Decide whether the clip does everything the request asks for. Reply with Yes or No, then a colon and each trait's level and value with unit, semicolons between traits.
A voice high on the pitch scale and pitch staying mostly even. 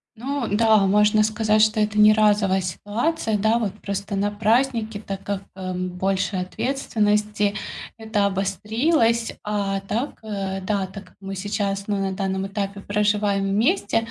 Yes: high, 205 Hz; narrow, 1.9 semitones